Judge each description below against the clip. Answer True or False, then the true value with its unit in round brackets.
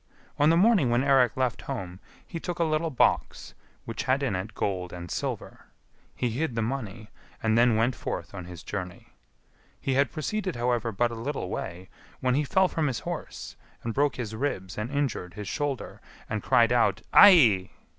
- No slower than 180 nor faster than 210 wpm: True (185 wpm)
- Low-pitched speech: True (120 Hz)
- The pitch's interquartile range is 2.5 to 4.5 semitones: False (5.1 semitones)